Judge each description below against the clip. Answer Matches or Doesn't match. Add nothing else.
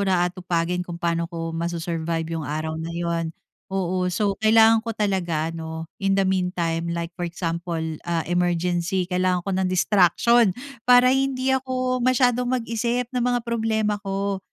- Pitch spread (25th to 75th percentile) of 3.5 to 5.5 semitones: Matches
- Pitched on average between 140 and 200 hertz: Matches